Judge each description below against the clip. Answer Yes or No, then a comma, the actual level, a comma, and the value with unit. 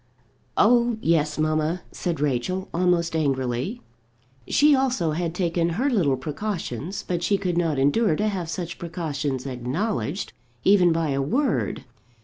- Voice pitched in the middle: Yes, medium, 170 Hz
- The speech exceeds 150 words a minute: No, slow, 135 wpm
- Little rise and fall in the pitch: No, average, 4.8 semitones